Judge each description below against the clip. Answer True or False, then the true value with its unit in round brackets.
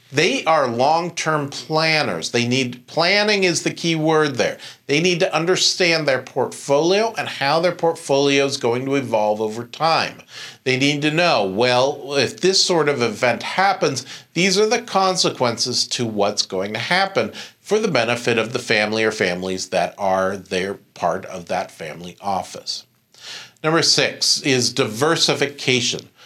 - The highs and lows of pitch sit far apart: True (5.8 semitones)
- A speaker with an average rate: True (155 wpm)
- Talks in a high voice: False (140 Hz)